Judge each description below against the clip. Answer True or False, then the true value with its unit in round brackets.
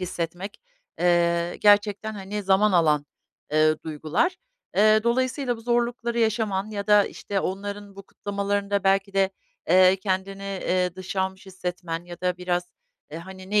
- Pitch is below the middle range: False (195 Hz)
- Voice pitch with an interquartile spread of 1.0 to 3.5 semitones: True (2.4 semitones)